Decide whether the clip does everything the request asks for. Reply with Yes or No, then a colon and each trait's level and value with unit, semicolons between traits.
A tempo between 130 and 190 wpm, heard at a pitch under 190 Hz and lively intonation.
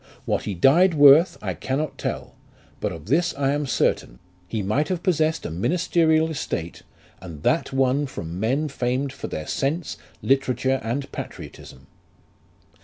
Yes: average, 150 wpm; low, 135 Hz; wide, 5.8 semitones